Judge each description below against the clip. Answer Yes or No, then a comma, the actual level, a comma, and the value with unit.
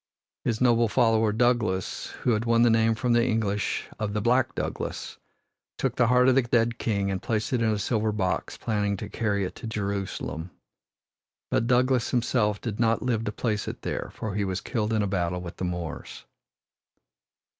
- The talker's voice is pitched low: Yes, low, 110 Hz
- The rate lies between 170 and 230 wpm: Yes, average, 190 wpm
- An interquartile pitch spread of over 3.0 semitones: No, average, 2.7 semitones